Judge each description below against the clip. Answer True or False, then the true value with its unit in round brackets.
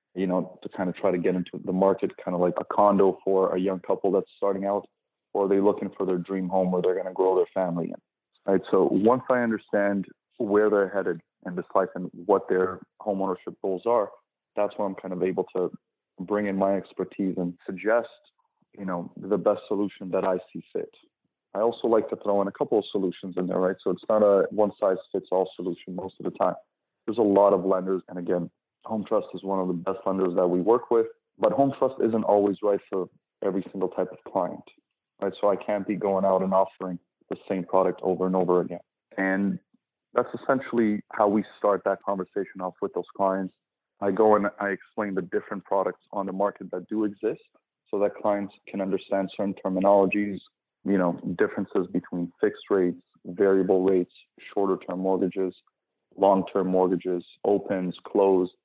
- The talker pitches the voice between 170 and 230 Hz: False (95 Hz)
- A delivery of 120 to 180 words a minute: False (205 wpm)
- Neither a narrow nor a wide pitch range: False (1.6 semitones)